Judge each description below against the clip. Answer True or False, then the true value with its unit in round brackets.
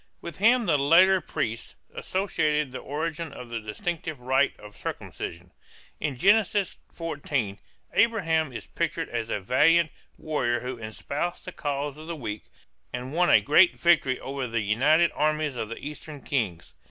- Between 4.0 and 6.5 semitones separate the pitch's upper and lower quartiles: True (5.1 semitones)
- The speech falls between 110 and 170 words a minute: True (155 wpm)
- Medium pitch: True (145 Hz)